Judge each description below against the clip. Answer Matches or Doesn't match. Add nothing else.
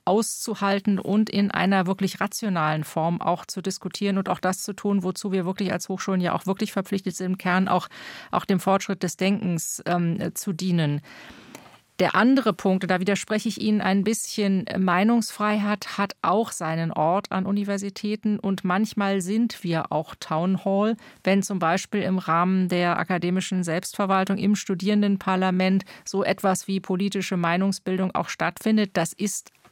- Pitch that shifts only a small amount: Matches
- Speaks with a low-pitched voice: Doesn't match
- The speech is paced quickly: Doesn't match